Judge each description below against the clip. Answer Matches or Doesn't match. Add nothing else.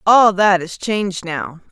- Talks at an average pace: Matches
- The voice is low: Doesn't match